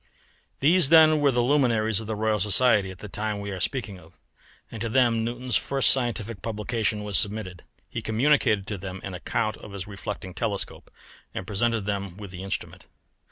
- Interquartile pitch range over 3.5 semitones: No, average, 3.2 semitones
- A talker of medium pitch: No, low, 110 Hz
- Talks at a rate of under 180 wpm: No, average, 185 wpm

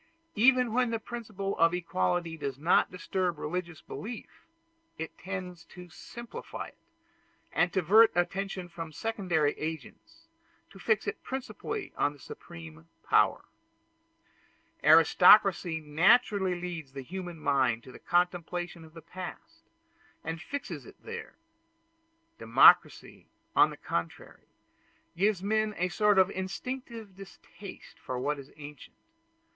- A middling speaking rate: No, slow, 125 wpm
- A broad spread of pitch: No, average, 4.5 semitones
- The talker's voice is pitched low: No, medium, 180 Hz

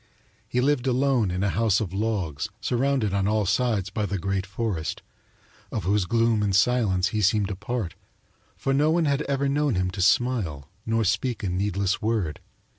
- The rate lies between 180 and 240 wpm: Yes, average, 185 wpm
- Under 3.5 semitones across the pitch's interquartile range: No, average, 4.4 semitones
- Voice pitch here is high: No, low, 105 Hz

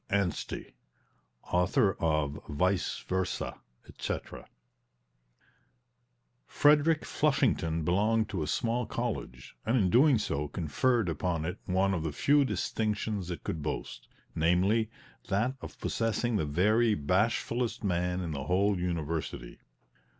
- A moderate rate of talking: No, slow, 120 wpm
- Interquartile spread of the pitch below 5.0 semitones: No, average, 5.3 semitones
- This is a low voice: Yes, very low, 95 Hz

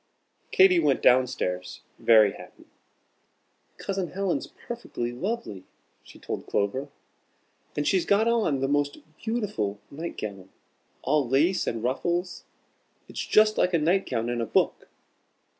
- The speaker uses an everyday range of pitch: No, wide, 8.0 semitones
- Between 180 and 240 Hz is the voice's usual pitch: No, medium, 145 Hz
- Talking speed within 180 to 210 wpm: No, slow, 135 wpm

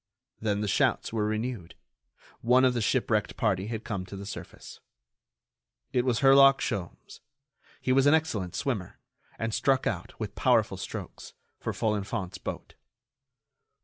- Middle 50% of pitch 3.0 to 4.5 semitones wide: Yes, average, 4.1 semitones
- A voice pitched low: Yes, low, 110 Hz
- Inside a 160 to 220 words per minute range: No, average, 145 wpm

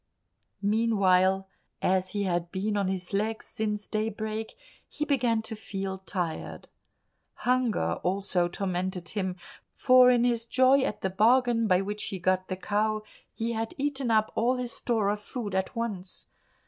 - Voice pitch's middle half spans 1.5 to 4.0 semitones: Yes, average, 3.5 semitones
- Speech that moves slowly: No, average, 155 wpm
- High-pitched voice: Yes, high, 210 Hz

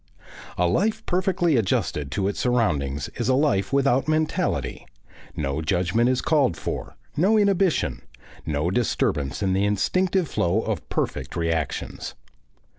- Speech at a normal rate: No, slow, 130 wpm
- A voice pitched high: No, low, 115 Hz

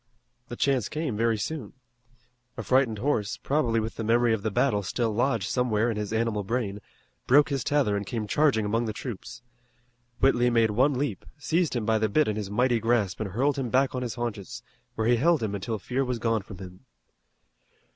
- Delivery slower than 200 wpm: No, fast, 205 wpm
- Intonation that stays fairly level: No, average, 3.4 semitones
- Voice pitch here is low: Yes, low, 115 Hz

